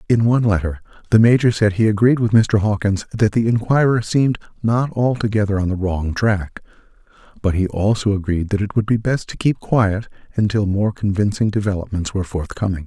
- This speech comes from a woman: No, male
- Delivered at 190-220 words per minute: No, average, 180 wpm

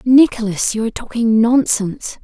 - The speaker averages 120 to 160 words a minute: Yes, slow, 135 wpm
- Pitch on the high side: Yes, high, 230 Hz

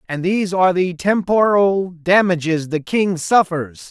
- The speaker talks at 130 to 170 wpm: Yes, average, 140 wpm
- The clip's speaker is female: No, male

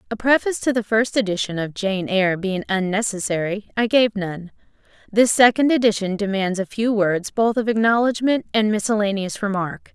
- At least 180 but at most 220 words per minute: No, average, 165 wpm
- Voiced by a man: No, female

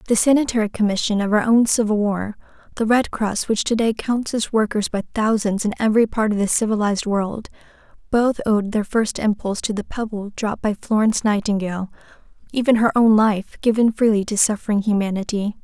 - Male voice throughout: No, female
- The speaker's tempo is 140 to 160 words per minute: No, average, 175 wpm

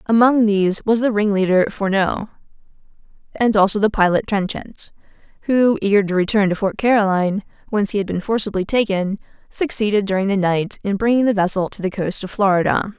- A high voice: Yes, high, 205 Hz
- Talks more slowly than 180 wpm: Yes, average, 170 wpm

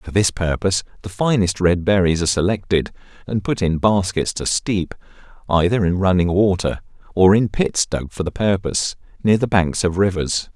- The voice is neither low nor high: No, very low, 95 Hz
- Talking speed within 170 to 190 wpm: Yes, average, 175 wpm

